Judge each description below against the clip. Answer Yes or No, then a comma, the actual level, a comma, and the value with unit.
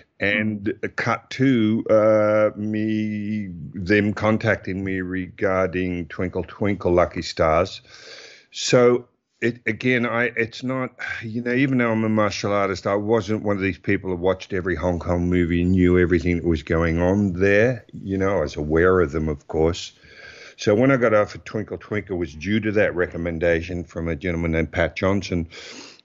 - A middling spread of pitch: Yes, average, 3.6 semitones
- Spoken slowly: No, average, 175 wpm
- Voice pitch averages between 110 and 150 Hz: No, low, 100 Hz